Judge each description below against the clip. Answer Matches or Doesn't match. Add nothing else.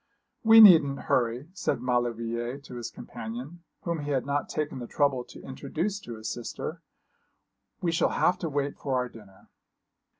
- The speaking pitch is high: Doesn't match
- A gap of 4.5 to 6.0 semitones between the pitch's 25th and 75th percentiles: Matches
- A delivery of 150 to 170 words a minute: Matches